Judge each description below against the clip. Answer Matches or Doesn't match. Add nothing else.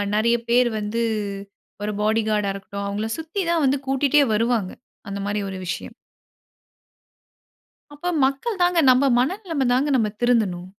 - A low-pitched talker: Doesn't match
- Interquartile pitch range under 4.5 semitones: Doesn't match